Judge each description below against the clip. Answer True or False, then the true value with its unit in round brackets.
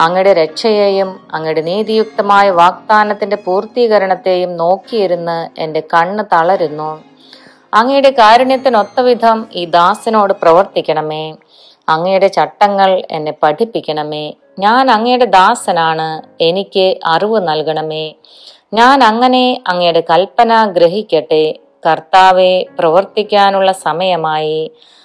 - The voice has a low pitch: False (185 Hz)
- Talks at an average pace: True (80 wpm)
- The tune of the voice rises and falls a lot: False (4.8 semitones)